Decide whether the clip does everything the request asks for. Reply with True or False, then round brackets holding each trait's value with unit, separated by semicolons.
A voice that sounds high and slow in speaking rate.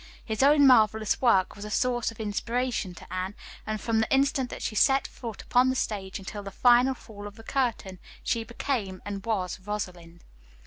False (220 Hz; 190 wpm)